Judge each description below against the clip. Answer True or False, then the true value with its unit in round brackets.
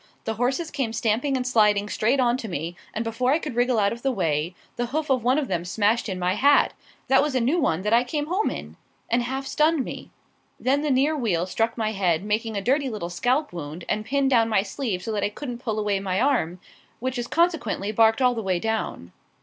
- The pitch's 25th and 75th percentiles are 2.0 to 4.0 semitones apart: False (4.6 semitones)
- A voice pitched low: False (230 Hz)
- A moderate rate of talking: False (240 wpm)